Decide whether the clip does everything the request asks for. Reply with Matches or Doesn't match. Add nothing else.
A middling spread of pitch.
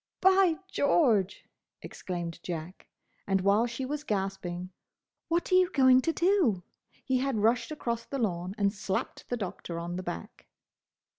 Doesn't match